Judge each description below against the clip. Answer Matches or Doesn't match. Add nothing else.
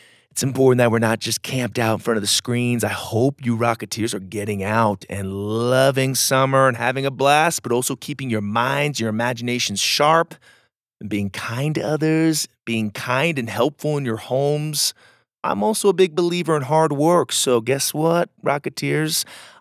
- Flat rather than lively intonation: Doesn't match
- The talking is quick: Doesn't match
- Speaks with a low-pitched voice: Matches